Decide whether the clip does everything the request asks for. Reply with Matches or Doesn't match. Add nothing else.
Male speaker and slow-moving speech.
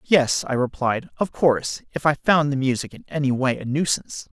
Doesn't match